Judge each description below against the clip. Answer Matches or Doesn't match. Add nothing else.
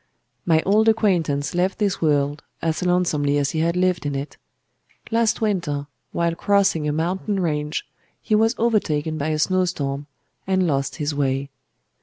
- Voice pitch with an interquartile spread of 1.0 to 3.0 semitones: Doesn't match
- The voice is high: Doesn't match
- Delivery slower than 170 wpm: Matches